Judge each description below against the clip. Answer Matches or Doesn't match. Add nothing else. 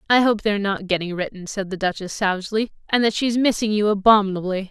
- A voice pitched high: Matches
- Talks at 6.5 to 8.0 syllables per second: Matches